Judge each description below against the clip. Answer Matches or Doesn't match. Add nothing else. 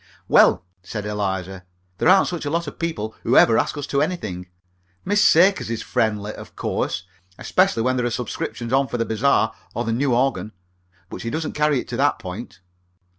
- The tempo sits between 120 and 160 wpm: Doesn't match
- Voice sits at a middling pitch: Doesn't match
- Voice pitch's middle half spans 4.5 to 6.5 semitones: Matches